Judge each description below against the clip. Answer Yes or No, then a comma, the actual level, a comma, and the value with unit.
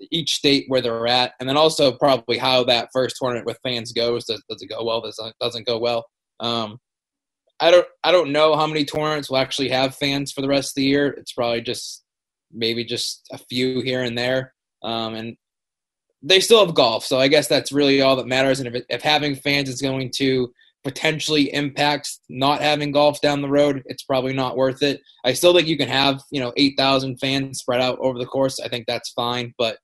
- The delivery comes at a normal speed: No, fast, 225 wpm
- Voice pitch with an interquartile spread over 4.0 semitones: No, narrow, 2.6 semitones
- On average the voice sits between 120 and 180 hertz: Yes, low, 130 Hz